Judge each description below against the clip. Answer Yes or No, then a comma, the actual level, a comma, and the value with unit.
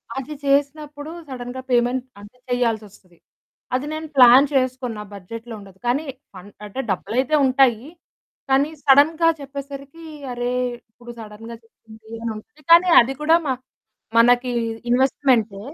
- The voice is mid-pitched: No, very high, 250 Hz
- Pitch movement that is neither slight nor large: Yes, average, 3.6 semitones